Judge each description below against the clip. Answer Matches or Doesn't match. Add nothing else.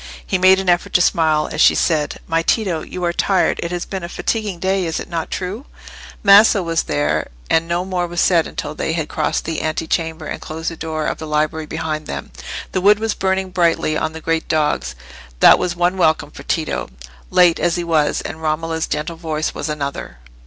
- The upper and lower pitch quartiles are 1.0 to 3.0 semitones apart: Matches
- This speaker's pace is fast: Matches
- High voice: Doesn't match